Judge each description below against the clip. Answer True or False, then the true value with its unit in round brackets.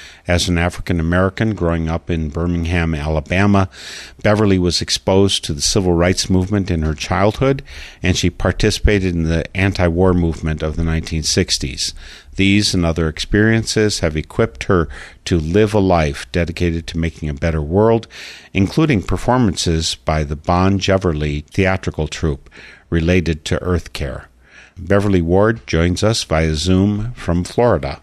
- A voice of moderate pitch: False (90 Hz)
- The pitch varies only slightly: False (3.3 semitones)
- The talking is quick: False (145 wpm)